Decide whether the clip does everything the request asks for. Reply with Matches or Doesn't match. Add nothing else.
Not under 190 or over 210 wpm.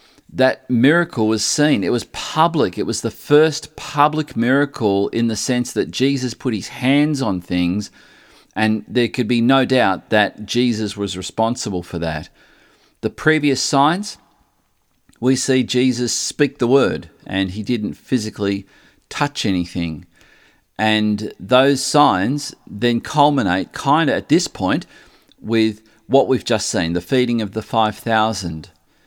Doesn't match